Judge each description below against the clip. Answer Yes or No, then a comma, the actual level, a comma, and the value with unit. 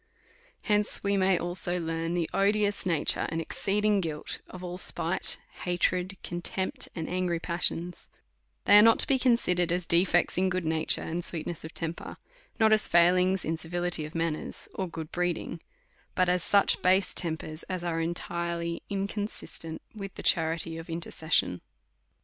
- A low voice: No, medium, 175 Hz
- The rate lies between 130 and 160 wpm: Yes, average, 155 wpm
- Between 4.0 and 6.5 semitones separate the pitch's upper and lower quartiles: No, narrow, 2.4 semitones